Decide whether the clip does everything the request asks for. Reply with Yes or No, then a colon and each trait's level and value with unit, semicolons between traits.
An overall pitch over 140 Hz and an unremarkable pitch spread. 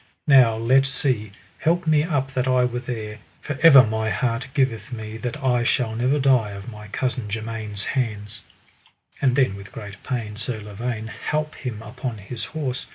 No: low, 120 Hz; average, 3.4 semitones